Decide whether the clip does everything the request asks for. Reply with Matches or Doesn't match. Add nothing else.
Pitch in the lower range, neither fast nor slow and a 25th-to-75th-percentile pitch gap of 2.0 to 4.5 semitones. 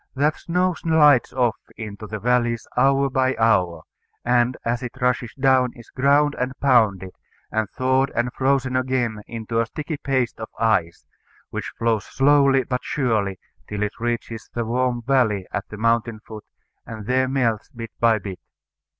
Matches